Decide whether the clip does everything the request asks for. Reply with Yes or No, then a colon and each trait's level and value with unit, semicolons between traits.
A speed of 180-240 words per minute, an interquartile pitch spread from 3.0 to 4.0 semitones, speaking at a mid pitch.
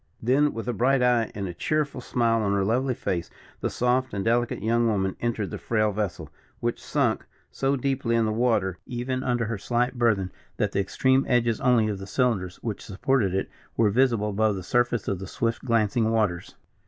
No: average, 200 wpm; average, 3.5 semitones; low, 115 Hz